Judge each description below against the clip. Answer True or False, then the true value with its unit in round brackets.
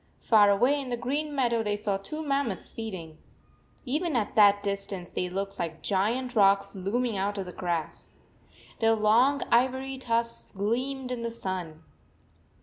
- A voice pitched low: False (220 Hz)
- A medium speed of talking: True (155 wpm)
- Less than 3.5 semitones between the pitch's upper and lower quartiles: False (4.3 semitones)